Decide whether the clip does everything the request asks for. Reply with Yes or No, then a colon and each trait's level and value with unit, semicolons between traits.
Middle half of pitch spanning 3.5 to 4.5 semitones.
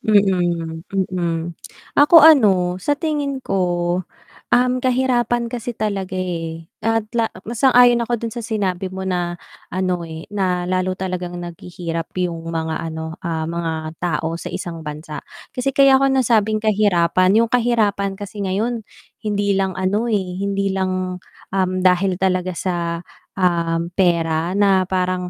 Yes: average, 4.0 semitones